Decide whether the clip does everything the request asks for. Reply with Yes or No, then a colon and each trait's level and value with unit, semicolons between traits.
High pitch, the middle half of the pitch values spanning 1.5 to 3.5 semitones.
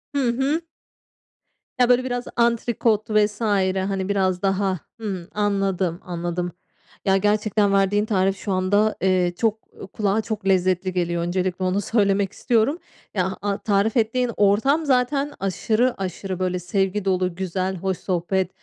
Yes: high, 195 Hz; average, 2.7 semitones